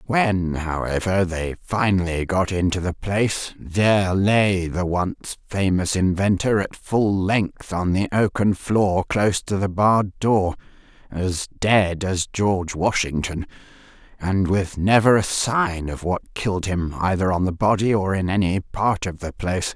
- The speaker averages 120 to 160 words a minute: Yes, average, 155 wpm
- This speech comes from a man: No, female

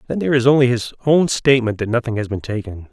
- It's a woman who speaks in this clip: No, male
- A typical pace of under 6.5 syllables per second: No, 6.9 syllables/s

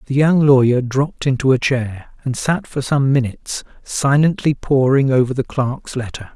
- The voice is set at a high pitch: No, low, 135 Hz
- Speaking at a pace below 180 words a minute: Yes, average, 170 wpm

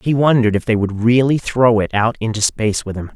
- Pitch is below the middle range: Yes, low, 115 Hz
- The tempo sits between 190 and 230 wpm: No, fast, 245 wpm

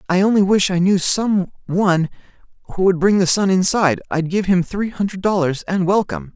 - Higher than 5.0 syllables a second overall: Yes, 5.5 syllables/s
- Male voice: Yes, male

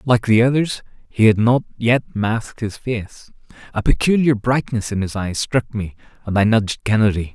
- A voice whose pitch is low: Yes, low, 115 Hz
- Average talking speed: Yes, average, 180 wpm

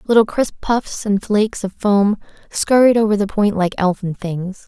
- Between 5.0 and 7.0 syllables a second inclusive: No, 4.6 syllables/s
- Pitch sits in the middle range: No, high, 205 Hz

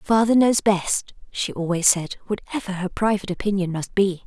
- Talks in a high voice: Yes, high, 195 Hz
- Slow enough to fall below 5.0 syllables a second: No, 5.1 syllables/s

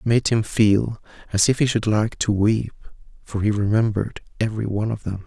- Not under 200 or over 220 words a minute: Yes, fast, 205 wpm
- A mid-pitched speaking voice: No, low, 110 Hz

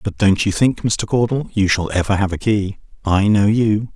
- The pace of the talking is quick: Yes, fast, 230 wpm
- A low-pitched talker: Yes, low, 105 Hz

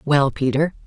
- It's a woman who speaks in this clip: Yes, female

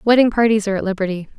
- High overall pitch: Yes, high, 210 Hz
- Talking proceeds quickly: Yes, fast, 215 wpm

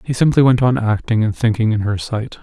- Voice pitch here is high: No, low, 115 Hz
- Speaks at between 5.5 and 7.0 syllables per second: Yes, 5.6 syllables/s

